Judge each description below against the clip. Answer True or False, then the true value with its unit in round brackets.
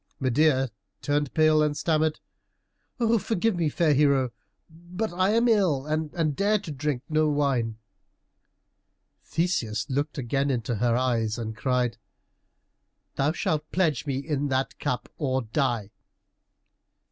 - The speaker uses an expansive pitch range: False (3.6 semitones)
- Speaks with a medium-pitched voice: True (145 Hz)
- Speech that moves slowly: True (125 wpm)